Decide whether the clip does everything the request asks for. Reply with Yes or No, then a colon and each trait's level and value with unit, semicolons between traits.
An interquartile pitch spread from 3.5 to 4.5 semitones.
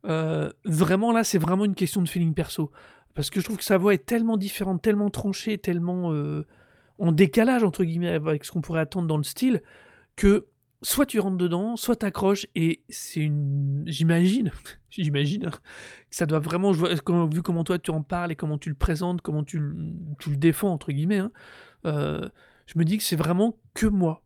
Yes: average, 3.9 semitones